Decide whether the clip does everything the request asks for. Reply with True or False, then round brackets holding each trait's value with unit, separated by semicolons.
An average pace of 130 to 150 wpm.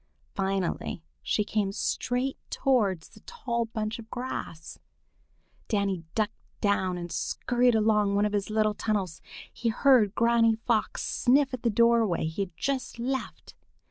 True (140 wpm)